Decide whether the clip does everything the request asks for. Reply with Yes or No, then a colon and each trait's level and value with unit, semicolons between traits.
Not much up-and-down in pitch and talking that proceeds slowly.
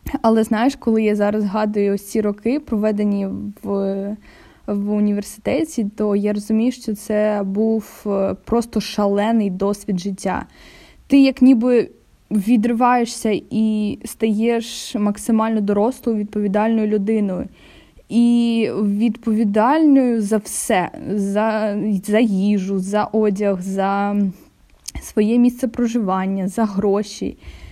Yes: narrow, 2.0 semitones; slow, 100 wpm